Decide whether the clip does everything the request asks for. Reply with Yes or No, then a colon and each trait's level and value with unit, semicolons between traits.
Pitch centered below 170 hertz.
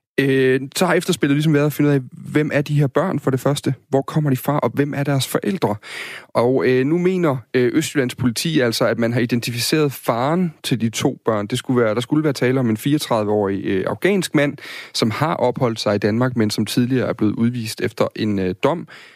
Yes: low, 135 Hz